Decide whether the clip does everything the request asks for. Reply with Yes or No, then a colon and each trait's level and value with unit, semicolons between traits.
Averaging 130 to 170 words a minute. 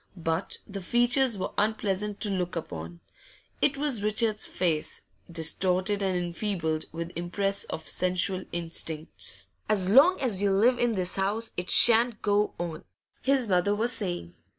Yes: average, 150 wpm